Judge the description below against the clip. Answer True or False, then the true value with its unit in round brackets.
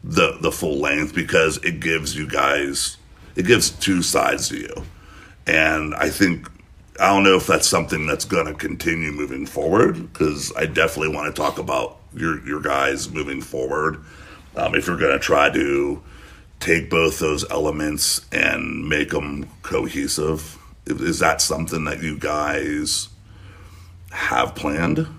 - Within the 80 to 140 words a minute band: False (155 wpm)